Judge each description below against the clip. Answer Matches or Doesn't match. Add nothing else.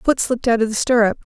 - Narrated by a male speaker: Doesn't match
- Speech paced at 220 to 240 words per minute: Doesn't match